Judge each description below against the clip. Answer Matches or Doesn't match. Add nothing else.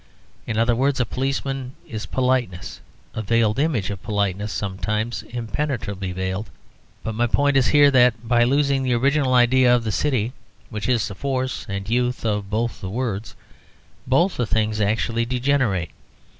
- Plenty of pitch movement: Doesn't match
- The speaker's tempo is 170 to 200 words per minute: Doesn't match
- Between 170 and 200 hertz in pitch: Doesn't match